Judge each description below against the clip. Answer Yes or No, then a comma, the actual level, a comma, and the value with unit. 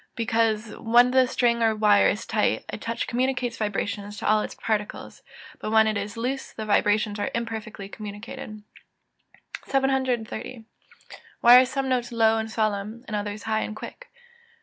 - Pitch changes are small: Yes, narrow, 2.3 semitones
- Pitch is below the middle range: No, high, 220 Hz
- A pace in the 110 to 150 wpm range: No, average, 165 wpm